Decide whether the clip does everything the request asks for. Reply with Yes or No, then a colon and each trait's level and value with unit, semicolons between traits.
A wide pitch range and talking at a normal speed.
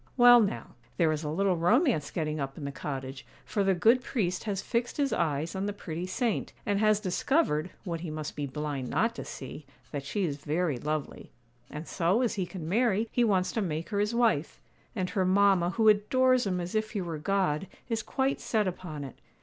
No: wide, 5.9 semitones; fast, 215 wpm